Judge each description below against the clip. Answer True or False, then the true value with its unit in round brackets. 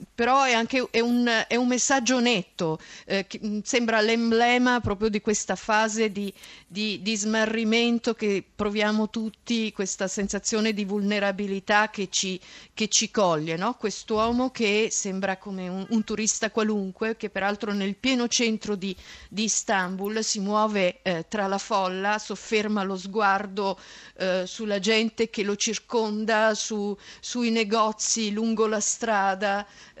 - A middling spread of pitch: False (2.0 semitones)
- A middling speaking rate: True (145 wpm)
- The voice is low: False (215 Hz)